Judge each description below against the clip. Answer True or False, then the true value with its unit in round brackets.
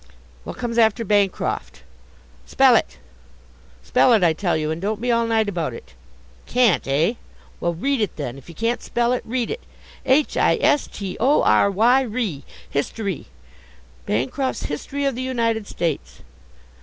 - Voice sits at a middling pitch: False (220 Hz)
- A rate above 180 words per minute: False (165 wpm)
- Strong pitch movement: True (6.3 semitones)